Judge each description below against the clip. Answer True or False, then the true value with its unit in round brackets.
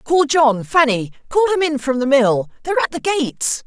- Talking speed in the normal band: True (195 wpm)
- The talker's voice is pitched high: True (280 Hz)